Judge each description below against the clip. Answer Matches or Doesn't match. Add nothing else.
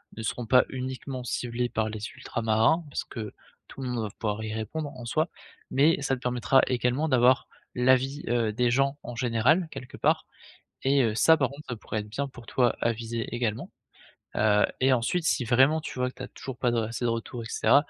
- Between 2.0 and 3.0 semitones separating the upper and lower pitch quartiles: Matches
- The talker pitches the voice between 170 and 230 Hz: Doesn't match